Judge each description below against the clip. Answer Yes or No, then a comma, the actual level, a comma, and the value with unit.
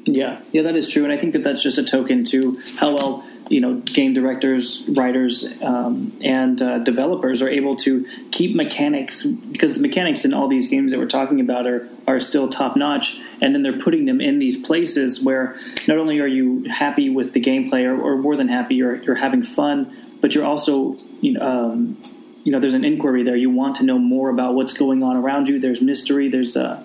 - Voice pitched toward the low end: No, medium, 155 Hz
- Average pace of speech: No, fast, 220 wpm